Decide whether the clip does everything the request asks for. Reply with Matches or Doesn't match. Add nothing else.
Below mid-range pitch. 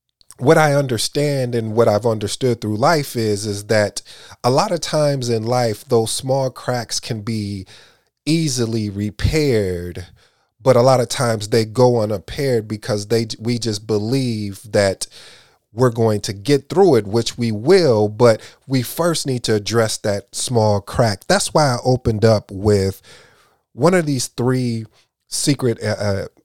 Matches